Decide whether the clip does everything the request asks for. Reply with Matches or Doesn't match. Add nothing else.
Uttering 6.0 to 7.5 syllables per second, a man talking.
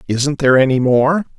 Doesn't match